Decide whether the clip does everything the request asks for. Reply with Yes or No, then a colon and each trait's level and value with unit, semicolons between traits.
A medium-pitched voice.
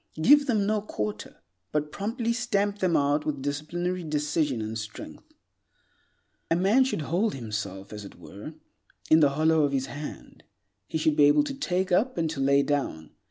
Yes: medium, 155 Hz